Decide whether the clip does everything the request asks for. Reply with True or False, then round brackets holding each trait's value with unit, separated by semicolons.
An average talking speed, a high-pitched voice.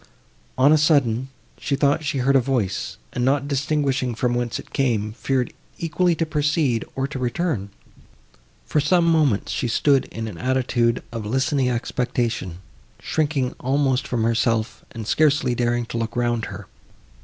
False (155 wpm; 130 Hz)